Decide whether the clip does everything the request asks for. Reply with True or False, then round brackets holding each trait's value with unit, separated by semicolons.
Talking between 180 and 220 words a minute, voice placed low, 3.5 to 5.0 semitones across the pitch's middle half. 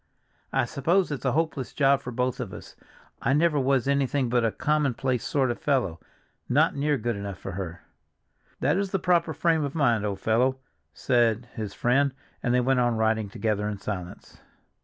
True (185 wpm; 125 Hz; 4.2 semitones)